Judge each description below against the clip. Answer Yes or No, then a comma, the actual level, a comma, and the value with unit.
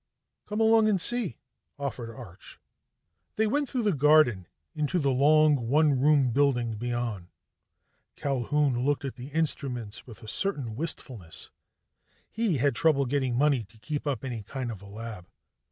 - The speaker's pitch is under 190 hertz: Yes, low, 135 Hz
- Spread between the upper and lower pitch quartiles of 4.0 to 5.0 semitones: Yes, average, 4.5 semitones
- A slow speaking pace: No, average, 155 wpm